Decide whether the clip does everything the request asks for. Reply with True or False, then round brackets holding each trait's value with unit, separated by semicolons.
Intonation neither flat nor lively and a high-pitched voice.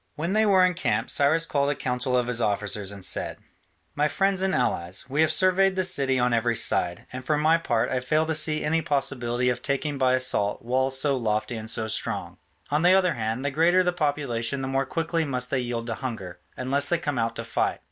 False (5.0 semitones; 135 Hz)